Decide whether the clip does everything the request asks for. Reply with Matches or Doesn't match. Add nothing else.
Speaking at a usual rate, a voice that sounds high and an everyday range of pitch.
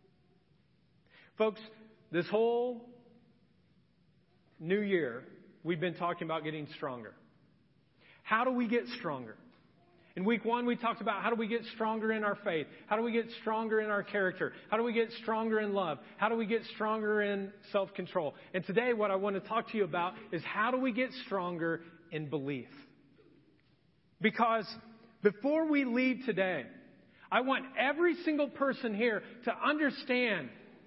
Matches